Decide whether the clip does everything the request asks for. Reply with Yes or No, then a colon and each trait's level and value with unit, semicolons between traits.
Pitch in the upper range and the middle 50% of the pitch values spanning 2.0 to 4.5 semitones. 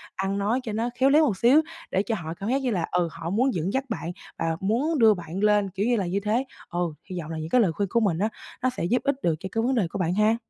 No: high, 205 Hz; average, 5.1 semitones